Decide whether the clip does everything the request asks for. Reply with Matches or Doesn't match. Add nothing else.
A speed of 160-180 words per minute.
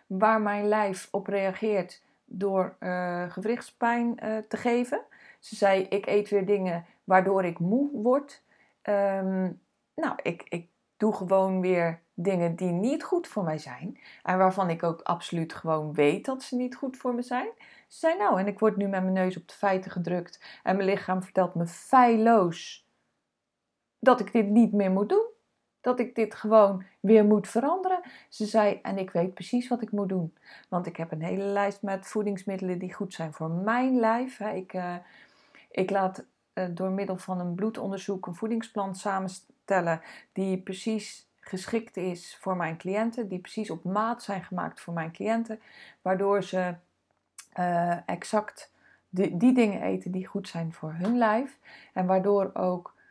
Matches